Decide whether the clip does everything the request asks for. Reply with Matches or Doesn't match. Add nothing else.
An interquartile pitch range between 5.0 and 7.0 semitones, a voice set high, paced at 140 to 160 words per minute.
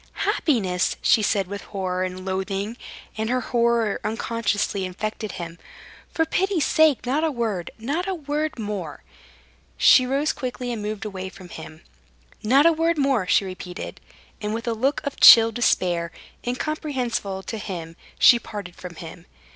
Matches